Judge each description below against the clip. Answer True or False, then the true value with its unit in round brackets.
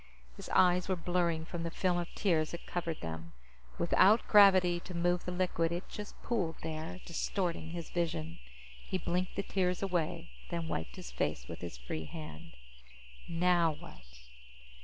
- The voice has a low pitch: False (170 Hz)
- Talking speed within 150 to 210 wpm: True (160 wpm)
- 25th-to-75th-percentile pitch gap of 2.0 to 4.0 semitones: True (2.4 semitones)